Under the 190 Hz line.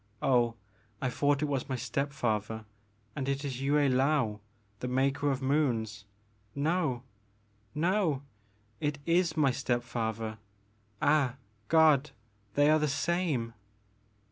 Yes: low, 135 Hz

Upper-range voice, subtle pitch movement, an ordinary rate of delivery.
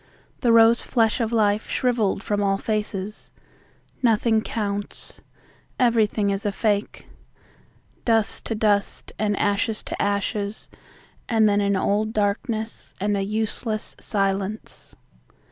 No: high, 210 Hz; narrow, 1.7 semitones; slow, 120 wpm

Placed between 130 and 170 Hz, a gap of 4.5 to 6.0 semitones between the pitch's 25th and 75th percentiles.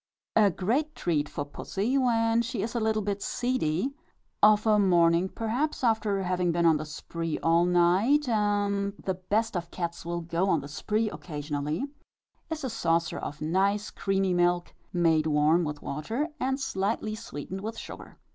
No: high, 190 Hz; average, 4.8 semitones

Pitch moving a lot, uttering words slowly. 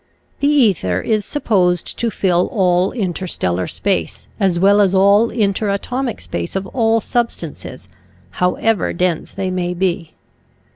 No: average, 3.9 semitones; slow, 130 wpm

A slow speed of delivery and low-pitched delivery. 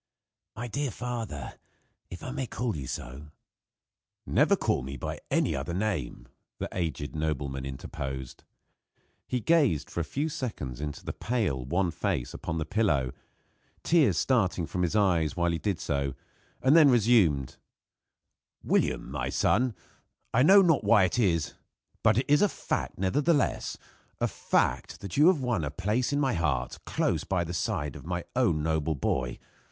No: average, 165 wpm; very low, 90 Hz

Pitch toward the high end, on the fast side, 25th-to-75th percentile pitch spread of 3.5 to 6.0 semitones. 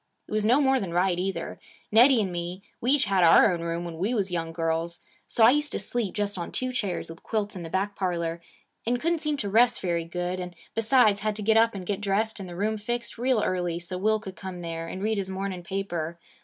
Yes: high, 195 Hz; fast, 250 wpm; average, 4.1 semitones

